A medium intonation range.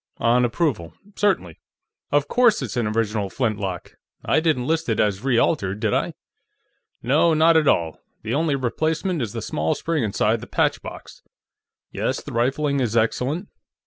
No: wide, 6.6 semitones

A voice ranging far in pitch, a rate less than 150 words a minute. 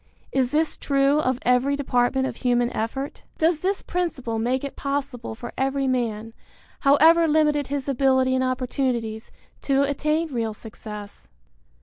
No: average, 2.8 semitones; average, 140 wpm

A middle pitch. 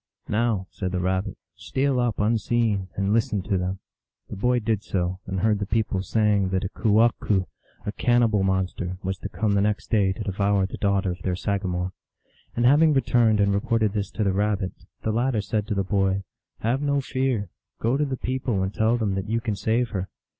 No: low, 105 Hz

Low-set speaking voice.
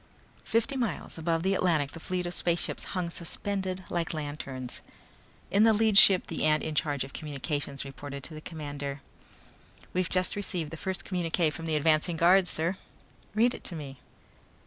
No: medium, 165 Hz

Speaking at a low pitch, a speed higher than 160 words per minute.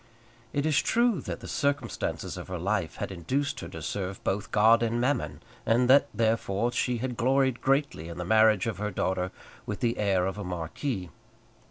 Yes: low, 110 Hz; average, 190 wpm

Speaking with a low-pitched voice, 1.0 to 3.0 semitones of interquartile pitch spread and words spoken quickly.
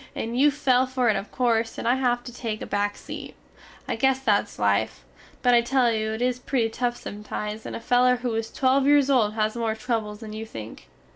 No: high, 230 Hz; average, 2.7 semitones; fast, 230 wpm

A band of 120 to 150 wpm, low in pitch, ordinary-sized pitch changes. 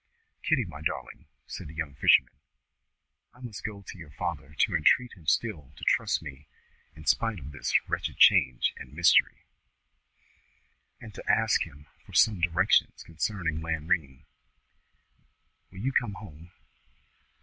No: average, 140 wpm; very low, 85 Hz; wide, 5.9 semitones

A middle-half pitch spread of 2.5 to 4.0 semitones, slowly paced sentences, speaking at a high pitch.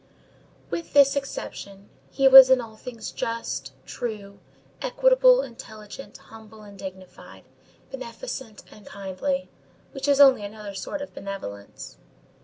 No: wide, 5.4 semitones; slow, 120 wpm; high, 230 Hz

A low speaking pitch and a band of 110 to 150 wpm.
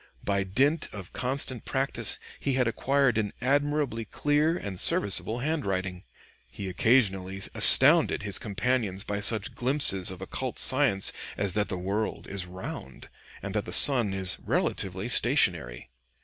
Yes: low, 105 Hz; average, 140 wpm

